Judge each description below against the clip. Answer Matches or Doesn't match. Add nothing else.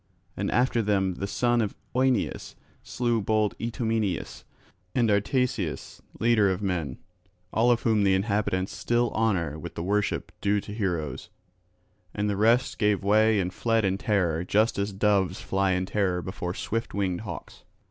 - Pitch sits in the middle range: Doesn't match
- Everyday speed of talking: Matches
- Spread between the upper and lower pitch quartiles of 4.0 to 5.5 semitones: Doesn't match